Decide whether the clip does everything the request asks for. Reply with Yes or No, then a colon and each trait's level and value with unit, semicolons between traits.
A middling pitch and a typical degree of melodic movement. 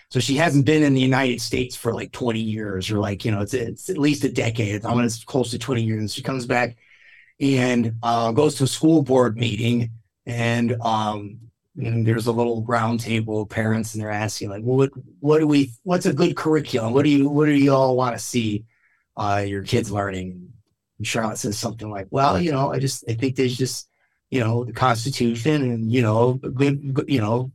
No: low, 120 Hz; average, 3.3 semitones